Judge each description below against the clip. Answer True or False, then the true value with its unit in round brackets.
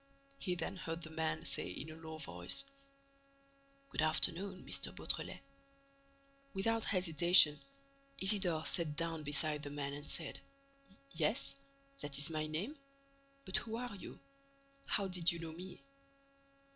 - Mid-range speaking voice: True (170 Hz)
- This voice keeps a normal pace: False (130 wpm)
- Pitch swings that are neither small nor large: True (4.2 semitones)